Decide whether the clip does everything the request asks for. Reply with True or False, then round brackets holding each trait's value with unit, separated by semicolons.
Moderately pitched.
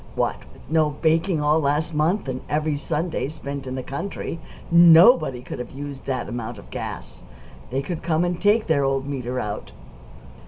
True (150 Hz)